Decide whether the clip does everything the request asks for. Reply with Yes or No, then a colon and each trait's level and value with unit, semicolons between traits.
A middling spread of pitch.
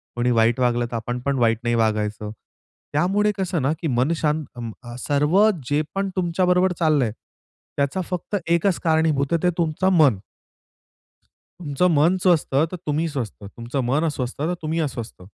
No: wide, 5.7 semitones